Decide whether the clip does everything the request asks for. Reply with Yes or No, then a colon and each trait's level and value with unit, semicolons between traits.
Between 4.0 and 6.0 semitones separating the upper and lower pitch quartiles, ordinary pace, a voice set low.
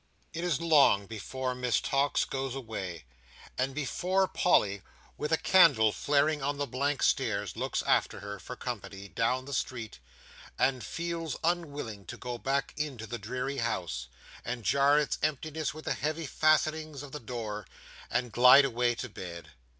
Yes: average, 4.8 semitones; average, 160 wpm; low, 130 Hz